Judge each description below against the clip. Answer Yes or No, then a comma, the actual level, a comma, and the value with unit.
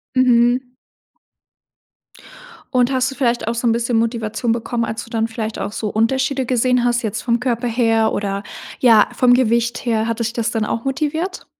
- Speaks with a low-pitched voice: No, high, 235 Hz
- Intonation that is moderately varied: No, narrow, 1.8 semitones